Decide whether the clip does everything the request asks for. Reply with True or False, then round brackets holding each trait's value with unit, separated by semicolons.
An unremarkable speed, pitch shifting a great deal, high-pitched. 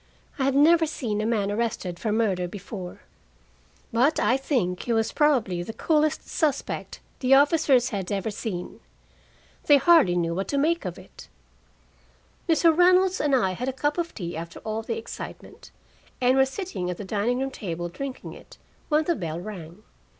True (175 wpm; 7.5 semitones; 235 Hz)